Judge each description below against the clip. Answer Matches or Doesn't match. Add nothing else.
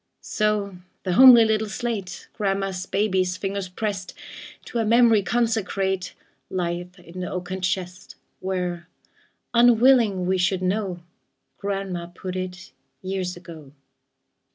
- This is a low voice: Doesn't match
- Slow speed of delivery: Matches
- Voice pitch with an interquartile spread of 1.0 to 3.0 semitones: Matches